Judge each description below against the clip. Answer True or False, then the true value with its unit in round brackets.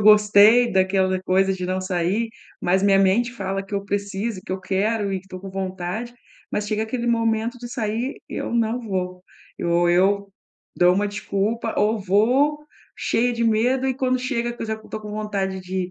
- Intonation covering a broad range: False (3.4 semitones)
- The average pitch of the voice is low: False (205 Hz)